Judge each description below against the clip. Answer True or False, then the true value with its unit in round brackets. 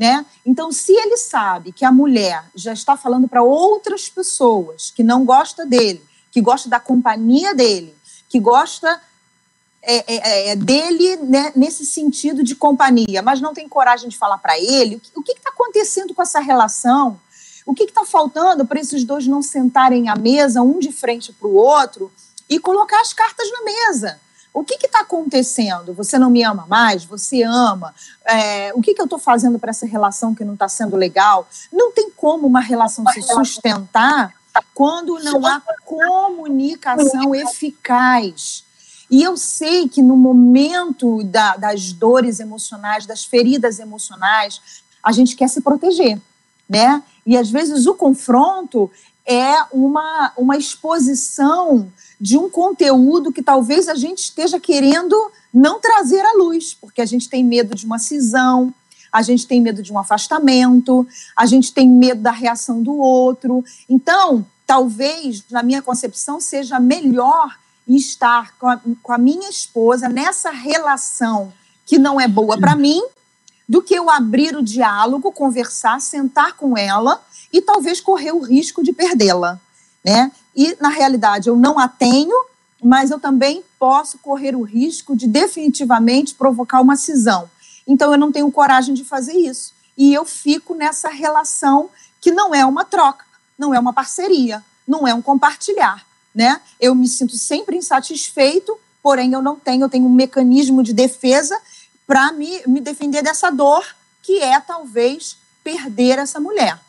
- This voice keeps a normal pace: True (160 wpm)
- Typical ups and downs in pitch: True (4.3 semitones)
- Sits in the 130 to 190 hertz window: False (265 Hz)